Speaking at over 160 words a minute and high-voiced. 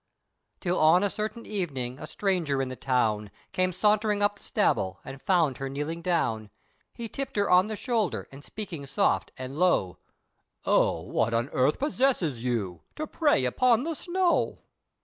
No: average, 170 wpm; medium, 175 Hz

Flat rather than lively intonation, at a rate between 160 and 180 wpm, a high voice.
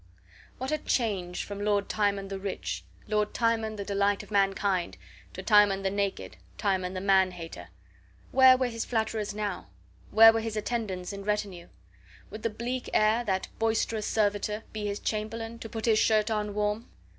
Yes: narrow, 2.1 semitones; average, 170 wpm; high, 210 Hz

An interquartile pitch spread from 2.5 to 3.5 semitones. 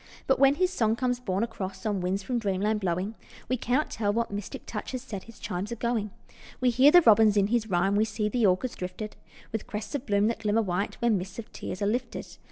Yes: average, 3.2 semitones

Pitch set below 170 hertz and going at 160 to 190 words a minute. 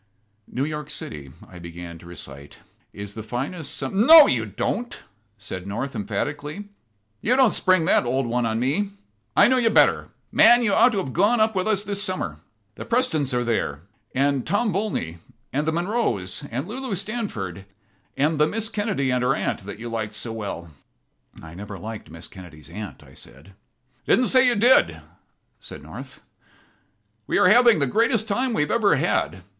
Yes: medium, 140 Hz; average, 185 wpm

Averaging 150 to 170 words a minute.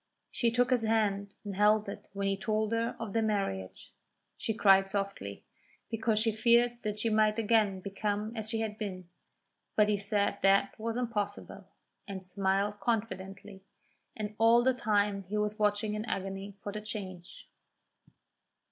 Yes: average, 160 wpm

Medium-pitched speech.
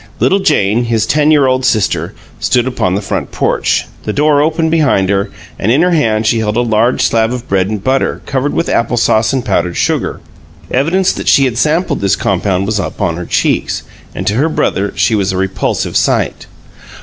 No: low, 115 Hz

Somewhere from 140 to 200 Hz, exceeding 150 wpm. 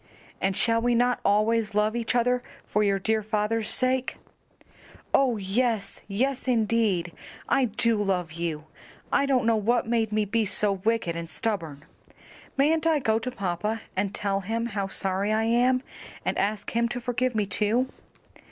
No: high, 220 Hz; average, 165 wpm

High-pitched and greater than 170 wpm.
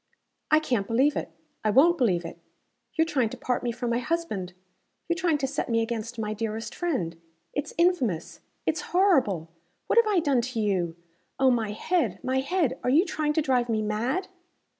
Yes: very high, 250 Hz; average, 190 wpm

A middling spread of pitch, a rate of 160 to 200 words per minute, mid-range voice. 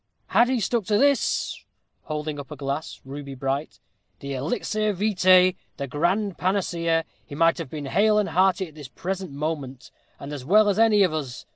No: wide, 6.0 semitones; average, 180 wpm; medium, 165 Hz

